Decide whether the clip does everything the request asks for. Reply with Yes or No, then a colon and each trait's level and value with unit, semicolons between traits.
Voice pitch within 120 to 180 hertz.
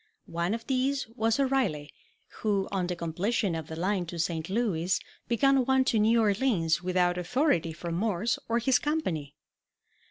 No: high, 200 Hz